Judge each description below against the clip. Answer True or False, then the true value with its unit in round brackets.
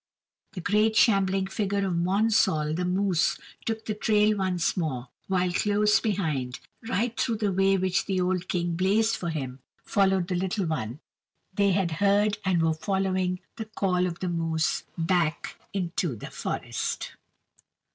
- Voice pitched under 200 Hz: True (185 Hz)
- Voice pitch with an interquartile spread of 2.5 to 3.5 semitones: True (3.0 semitones)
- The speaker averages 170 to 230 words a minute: False (155 wpm)